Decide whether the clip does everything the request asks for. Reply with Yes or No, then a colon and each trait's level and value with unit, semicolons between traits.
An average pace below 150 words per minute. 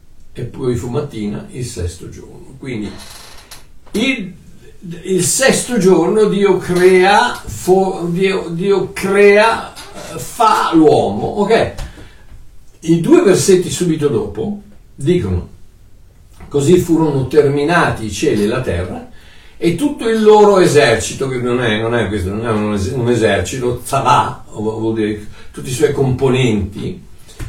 Yes: average, 125 wpm